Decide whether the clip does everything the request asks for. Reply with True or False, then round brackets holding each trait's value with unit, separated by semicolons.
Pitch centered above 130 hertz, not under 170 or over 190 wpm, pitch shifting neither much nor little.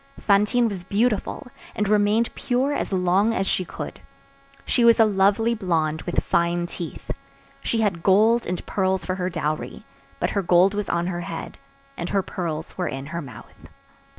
True (190 Hz; 175 wpm; 3.6 semitones)